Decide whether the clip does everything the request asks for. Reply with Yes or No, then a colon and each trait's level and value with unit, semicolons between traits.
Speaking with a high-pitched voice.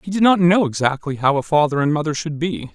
No: medium, 155 Hz